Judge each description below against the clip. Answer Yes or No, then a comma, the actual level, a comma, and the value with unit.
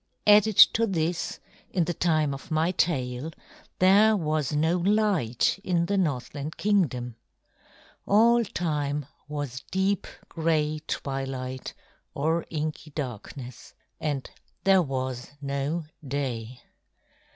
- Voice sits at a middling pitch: Yes, medium, 155 Hz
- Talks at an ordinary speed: No, slow, 105 wpm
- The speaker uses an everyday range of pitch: Yes, average, 4.9 semitones